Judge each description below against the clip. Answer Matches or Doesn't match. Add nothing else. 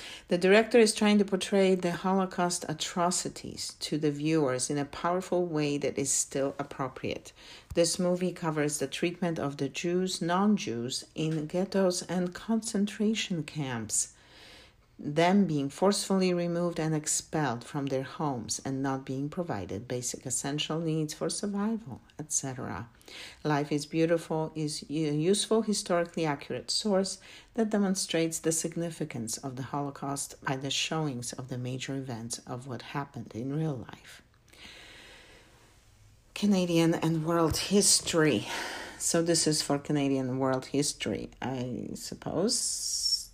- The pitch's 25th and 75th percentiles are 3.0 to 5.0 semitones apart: Matches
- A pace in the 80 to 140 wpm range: Matches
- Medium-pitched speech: Matches